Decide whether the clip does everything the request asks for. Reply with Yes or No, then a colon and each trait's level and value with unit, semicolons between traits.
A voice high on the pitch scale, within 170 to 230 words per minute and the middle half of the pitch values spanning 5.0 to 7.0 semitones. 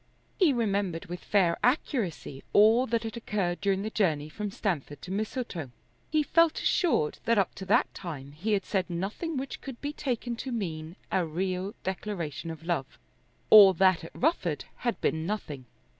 Yes: high, 195 Hz; average, 175 wpm; wide, 5.4 semitones